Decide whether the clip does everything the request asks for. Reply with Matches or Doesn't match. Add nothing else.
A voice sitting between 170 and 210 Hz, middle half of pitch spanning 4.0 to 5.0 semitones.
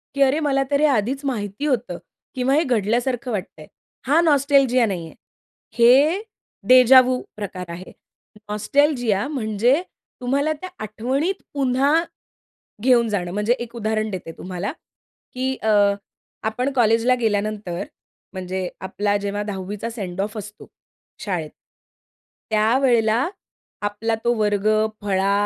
Doesn't match